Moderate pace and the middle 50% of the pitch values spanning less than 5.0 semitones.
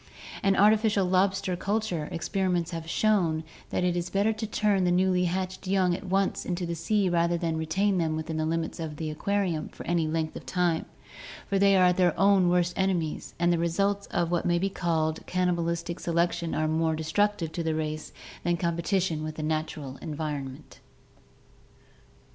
Yes: average, 175 wpm; average, 2.9 semitones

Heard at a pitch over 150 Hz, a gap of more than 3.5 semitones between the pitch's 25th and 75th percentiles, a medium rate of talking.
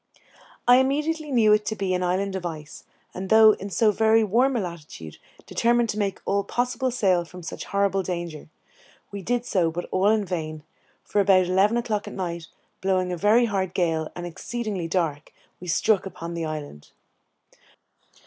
Yes: high, 190 Hz; average, 4.1 semitones; average, 175 wpm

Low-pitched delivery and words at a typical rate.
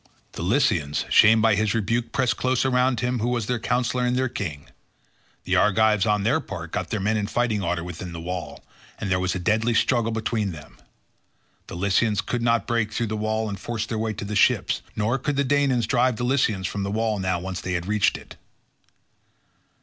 No: low, 110 Hz; fast, 215 wpm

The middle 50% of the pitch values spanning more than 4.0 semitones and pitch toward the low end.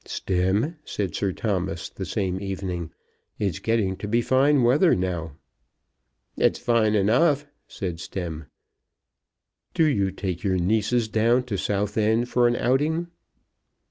Yes: average, 4.5 semitones; low, 105 Hz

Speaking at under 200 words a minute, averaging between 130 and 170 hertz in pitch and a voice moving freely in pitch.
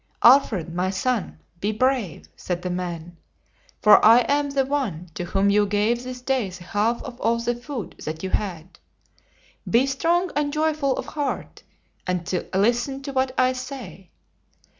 No: average, 160 wpm; high, 235 Hz; wide, 6.3 semitones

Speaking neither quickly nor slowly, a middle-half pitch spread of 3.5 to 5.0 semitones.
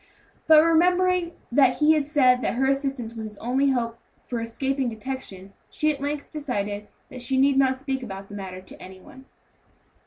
Yes: average, 185 wpm; average, 3.8 semitones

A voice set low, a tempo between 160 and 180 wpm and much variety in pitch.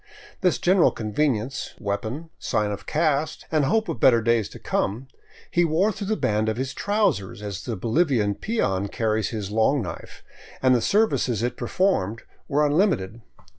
Yes: low, 125 Hz; average, 170 wpm; wide, 6.9 semitones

